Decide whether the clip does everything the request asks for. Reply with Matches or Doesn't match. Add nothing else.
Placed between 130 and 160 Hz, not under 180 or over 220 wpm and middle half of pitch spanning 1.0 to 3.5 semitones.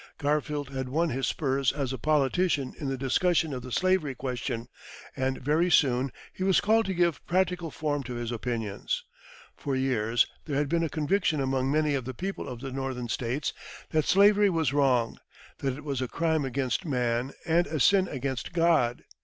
Doesn't match